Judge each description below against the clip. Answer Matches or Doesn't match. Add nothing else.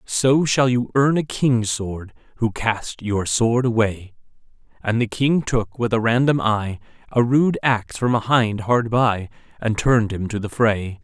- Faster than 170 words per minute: Matches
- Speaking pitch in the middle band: Doesn't match